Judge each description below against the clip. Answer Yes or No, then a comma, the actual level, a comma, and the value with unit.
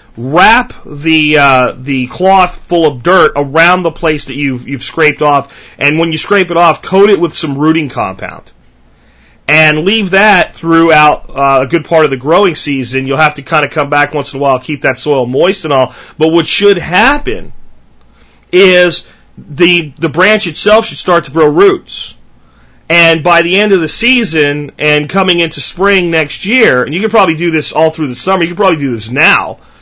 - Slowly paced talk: No, average, 200 wpm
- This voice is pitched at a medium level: Yes, medium, 160 Hz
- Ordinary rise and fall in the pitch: Yes, average, 3.9 semitones